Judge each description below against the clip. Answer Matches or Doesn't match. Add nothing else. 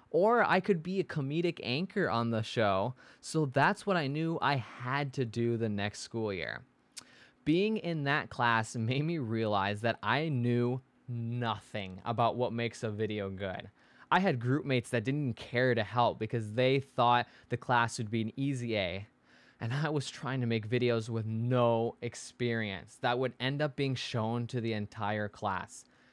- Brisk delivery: Doesn't match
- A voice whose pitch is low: Matches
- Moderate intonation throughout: Matches